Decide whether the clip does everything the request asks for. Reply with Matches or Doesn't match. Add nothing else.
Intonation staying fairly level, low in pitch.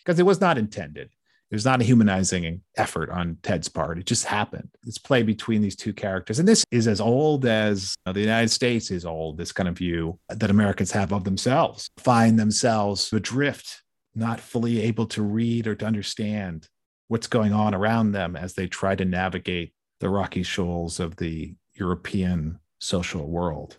Doesn't match